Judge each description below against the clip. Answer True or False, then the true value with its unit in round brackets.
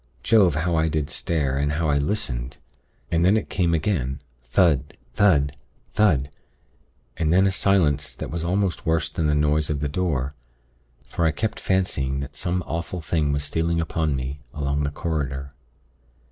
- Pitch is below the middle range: True (80 Hz)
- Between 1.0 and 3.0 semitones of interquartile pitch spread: False (3.4 semitones)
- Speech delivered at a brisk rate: False (170 wpm)